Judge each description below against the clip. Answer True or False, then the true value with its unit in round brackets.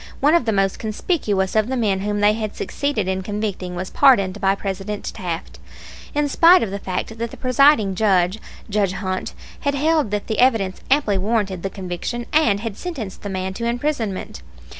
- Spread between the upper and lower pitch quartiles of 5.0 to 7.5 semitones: False (4.0 semitones)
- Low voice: False (210 Hz)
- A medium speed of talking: True (185 wpm)